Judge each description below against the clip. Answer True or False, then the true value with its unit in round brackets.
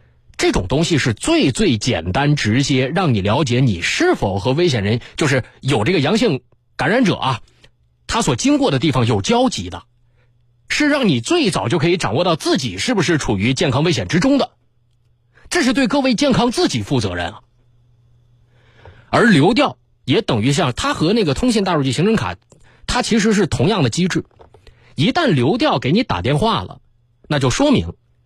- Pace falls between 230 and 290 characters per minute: True (265 characters per minute)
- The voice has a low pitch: True (130 Hz)